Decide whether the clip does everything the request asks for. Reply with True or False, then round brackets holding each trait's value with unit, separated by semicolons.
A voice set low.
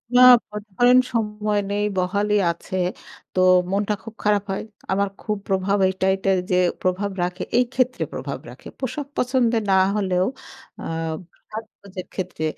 False (205 Hz)